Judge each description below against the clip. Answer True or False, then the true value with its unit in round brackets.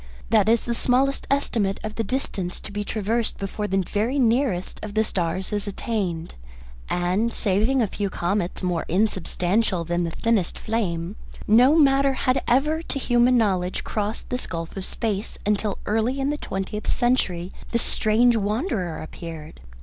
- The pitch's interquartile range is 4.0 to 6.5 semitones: True (4.4 semitones)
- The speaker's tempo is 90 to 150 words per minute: False (160 wpm)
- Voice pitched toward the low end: False (210 Hz)